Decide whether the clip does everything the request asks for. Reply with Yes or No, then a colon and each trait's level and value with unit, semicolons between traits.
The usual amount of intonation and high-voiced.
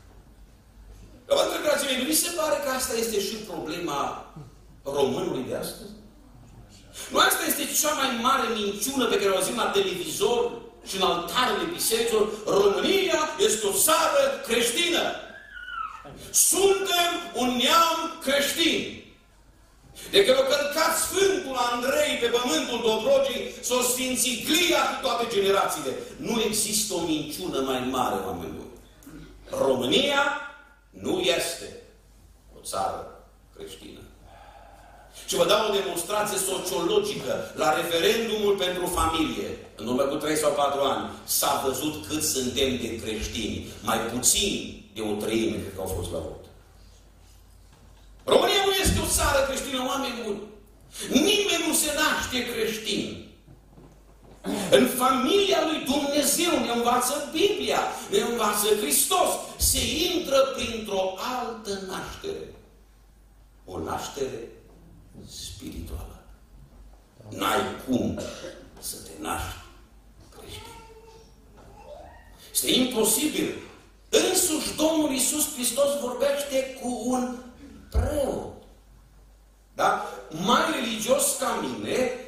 No: wide, 8.4 semitones; very high, 250 Hz